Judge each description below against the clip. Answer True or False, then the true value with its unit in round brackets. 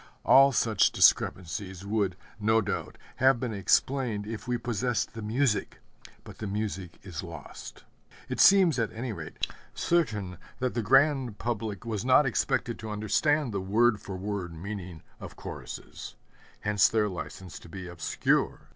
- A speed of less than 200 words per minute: True (150 wpm)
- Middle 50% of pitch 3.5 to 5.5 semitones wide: True (4.1 semitones)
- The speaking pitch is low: True (105 Hz)